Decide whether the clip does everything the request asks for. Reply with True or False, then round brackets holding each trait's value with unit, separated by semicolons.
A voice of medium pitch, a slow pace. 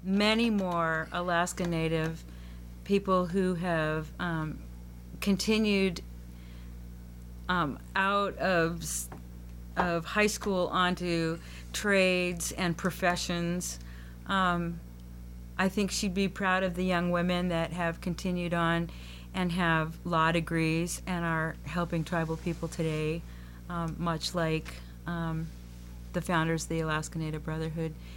True (165 Hz; 115 wpm)